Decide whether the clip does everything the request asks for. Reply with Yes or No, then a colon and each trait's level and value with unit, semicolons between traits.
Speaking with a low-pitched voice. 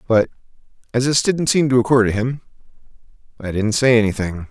Yes: low, 120 Hz